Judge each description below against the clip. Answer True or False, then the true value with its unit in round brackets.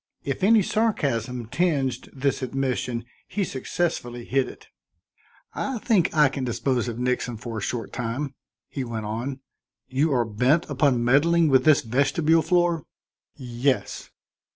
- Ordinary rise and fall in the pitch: True (4.4 semitones)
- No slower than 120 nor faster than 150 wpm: True (140 wpm)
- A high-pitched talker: False (135 Hz)